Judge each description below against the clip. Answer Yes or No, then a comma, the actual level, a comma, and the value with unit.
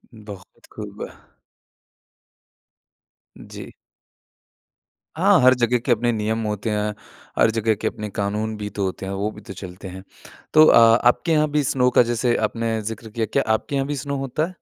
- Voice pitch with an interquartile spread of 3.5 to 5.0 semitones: No, average, 3.1 semitones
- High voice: No, low, 110 Hz